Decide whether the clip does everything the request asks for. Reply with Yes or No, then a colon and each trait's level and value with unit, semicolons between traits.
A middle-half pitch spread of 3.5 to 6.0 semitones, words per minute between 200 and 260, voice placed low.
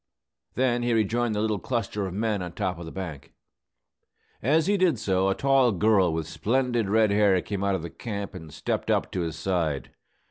Yes: average, 4.4 semitones; fast, 205 wpm; low, 100 Hz